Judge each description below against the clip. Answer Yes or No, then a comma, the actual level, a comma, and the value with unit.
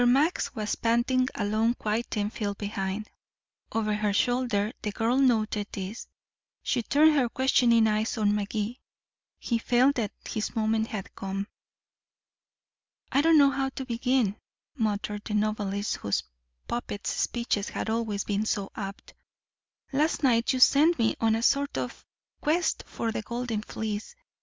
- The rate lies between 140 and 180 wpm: Yes, average, 145 wpm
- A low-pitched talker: No, high, 225 Hz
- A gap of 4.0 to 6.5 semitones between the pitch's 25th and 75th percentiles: No, average, 3.2 semitones